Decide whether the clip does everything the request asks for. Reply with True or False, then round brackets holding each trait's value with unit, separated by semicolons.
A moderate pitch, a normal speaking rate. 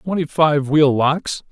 True (150 Hz; 160 wpm)